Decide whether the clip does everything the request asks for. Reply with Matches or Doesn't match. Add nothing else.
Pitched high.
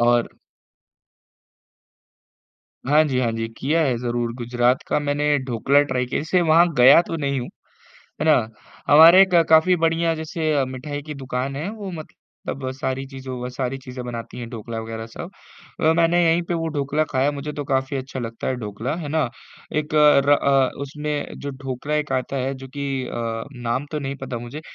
Doesn't match